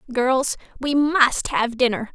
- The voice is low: No, very high, 260 Hz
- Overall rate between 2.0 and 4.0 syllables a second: Yes, 3.7 syllables/s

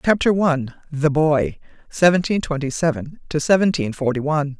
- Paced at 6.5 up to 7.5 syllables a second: No, 5.3 syllables/s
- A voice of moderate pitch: Yes, medium, 155 Hz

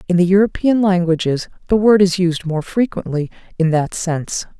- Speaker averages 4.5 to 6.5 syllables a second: Yes, 5.2 syllables/s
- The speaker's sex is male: No, female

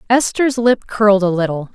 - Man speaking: No, female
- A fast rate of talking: No, average, 170 wpm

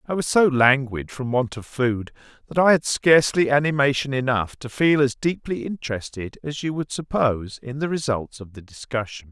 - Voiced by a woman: No, male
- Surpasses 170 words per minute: Yes, average, 185 wpm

